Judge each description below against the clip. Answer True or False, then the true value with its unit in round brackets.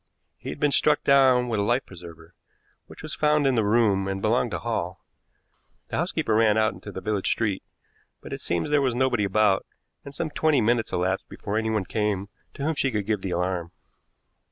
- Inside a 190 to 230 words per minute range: True (200 wpm)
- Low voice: True (110 Hz)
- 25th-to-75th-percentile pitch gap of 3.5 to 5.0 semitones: True (4.5 semitones)